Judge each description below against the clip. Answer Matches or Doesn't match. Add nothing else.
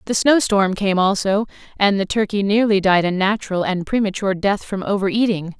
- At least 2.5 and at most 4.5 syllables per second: Doesn't match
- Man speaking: Doesn't match